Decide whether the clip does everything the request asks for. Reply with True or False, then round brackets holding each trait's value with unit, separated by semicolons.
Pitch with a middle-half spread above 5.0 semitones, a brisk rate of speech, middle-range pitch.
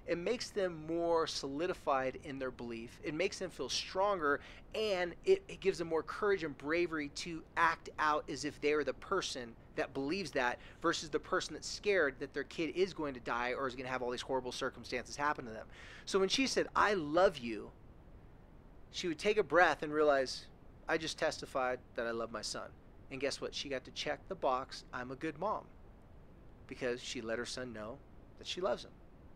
True (5.4 semitones; 210 wpm; 150 Hz)